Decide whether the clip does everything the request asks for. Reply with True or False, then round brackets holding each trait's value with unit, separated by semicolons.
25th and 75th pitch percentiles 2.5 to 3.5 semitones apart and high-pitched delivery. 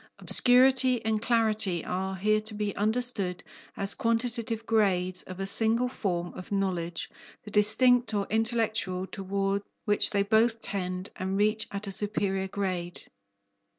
True (2.9 semitones; 205 Hz)